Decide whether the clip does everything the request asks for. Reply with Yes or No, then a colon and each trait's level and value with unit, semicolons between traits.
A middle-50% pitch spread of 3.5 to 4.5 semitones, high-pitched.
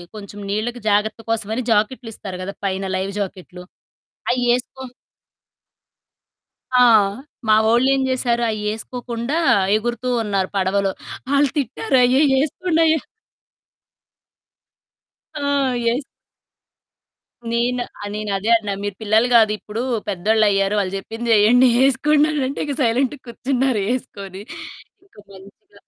Yes: average, 4.0 semitones; high, 230 Hz